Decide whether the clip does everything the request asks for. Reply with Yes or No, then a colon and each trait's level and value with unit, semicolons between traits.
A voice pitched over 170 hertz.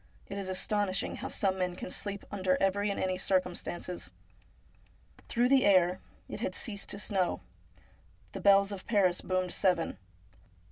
Yes: high, 190 Hz